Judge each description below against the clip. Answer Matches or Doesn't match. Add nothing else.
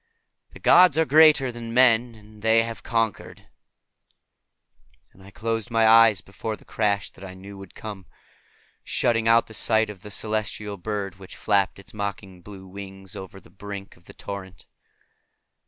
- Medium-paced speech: Matches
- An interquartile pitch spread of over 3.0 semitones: Doesn't match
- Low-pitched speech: Matches